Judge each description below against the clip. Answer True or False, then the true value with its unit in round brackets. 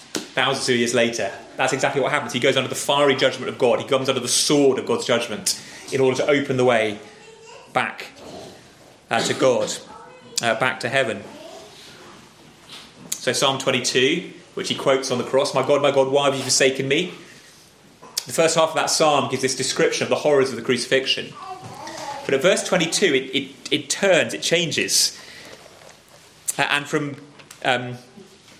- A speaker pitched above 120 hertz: True (135 Hz)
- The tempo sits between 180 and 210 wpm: True (185 wpm)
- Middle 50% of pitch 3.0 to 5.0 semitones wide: False (2.5 semitones)